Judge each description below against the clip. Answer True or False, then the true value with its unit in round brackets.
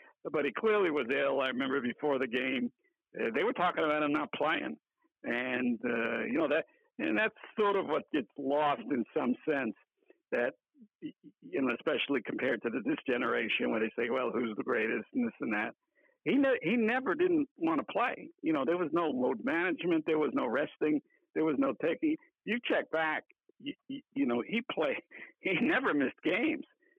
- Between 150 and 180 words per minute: False (195 wpm)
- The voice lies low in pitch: False (270 Hz)